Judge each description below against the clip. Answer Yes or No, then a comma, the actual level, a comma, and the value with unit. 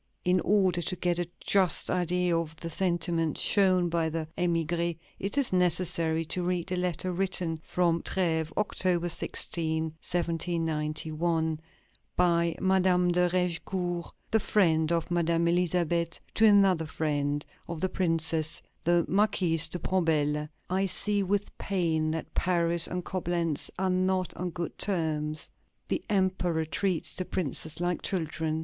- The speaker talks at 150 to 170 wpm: No, average, 140 wpm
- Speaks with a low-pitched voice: No, medium, 175 Hz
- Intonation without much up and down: Yes, narrow, 2.1 semitones